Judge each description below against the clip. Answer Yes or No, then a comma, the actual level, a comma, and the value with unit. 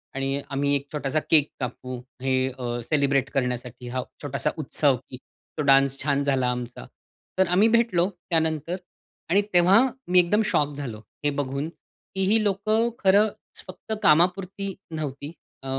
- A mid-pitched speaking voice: Yes, medium, 150 Hz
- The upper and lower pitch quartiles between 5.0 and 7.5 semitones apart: Yes, average, 5.3 semitones